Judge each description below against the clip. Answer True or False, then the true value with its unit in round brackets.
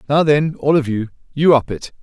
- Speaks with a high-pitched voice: False (145 Hz)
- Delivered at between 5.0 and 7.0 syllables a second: True (5.1 syllables/s)